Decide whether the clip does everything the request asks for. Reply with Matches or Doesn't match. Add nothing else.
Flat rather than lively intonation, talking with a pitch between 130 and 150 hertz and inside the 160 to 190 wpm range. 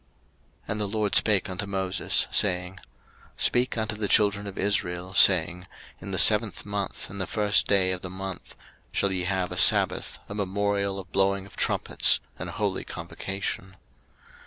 Doesn't match